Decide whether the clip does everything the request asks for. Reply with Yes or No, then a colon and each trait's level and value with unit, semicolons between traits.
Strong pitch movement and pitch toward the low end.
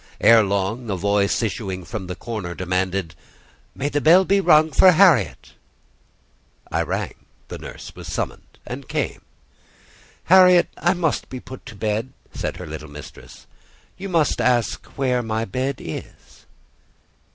Yes: wide, 8.1 semitones; low, 115 Hz